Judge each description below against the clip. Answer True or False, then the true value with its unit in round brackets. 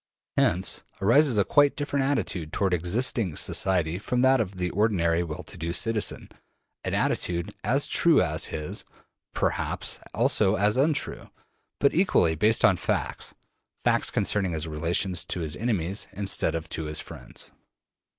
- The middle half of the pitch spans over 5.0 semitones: True (5.5 semitones)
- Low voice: True (95 Hz)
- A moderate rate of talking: True (150 wpm)